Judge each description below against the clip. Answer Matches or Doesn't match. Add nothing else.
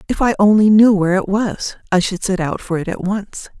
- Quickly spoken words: Matches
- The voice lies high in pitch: Matches